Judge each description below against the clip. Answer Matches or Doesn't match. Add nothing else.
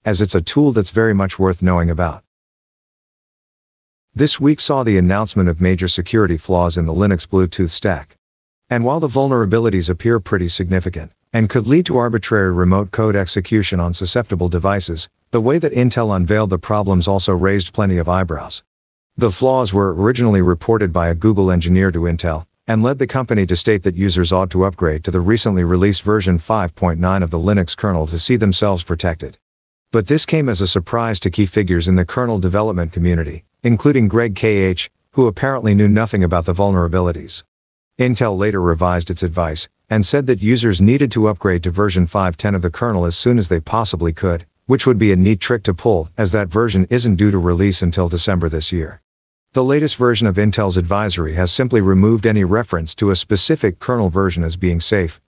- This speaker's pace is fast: Doesn't match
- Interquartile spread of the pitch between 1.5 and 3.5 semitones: Doesn't match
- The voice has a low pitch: Matches